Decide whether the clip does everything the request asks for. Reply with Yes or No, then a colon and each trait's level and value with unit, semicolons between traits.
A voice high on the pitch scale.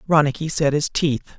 No: medium, 150 Hz